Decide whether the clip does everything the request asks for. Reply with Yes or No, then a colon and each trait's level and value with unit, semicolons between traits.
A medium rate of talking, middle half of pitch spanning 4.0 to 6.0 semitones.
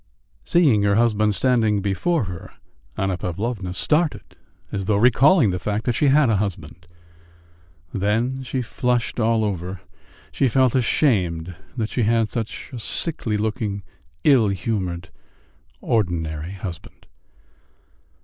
No: slow, 125 wpm; average, 4.4 semitones